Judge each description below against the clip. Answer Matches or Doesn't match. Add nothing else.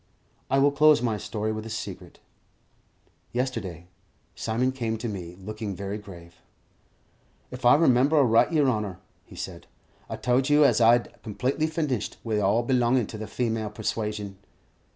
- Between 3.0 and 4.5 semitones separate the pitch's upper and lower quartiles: Matches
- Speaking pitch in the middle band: Doesn't match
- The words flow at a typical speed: Matches